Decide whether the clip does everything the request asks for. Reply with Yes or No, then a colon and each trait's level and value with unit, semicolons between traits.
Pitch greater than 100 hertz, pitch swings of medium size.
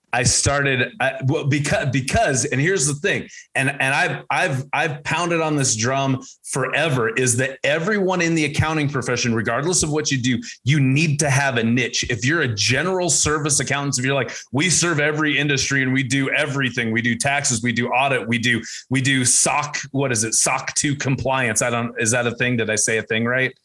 Yes: low, 135 Hz; average, 3.2 semitones